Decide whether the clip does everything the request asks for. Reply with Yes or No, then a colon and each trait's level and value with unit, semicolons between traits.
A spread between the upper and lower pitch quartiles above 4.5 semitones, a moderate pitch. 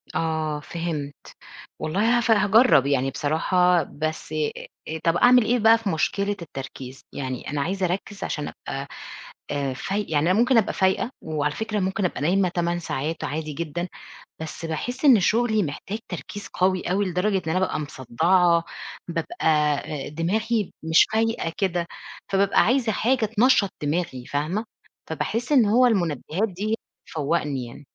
Yes: wide, 5.6 semitones; medium, 175 Hz